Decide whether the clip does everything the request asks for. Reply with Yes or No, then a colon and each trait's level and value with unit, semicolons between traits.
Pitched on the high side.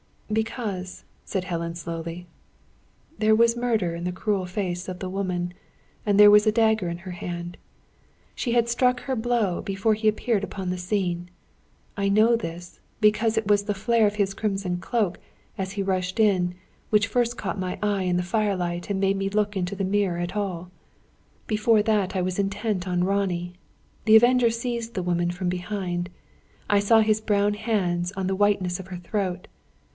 Yes: high, 195 Hz